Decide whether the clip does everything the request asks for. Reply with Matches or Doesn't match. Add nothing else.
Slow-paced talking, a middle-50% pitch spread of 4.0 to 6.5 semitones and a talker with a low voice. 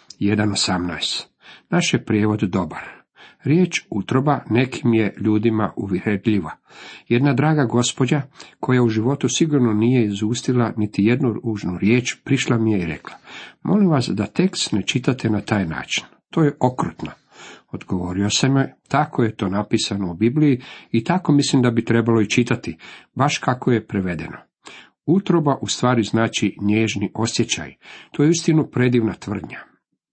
Doesn't match